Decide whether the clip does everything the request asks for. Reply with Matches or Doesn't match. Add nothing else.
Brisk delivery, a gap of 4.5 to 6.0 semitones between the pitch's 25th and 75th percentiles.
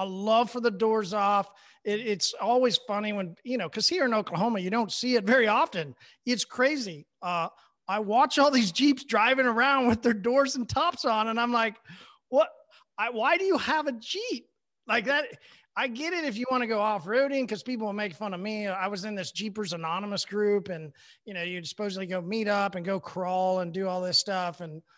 Matches